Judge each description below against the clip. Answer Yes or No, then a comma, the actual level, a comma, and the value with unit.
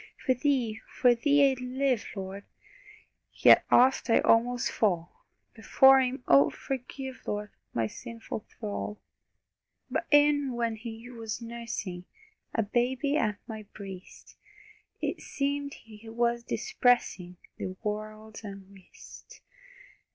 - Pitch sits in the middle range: No, high, 230 Hz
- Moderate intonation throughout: Yes, average, 3.7 semitones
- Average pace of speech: No, slow, 115 wpm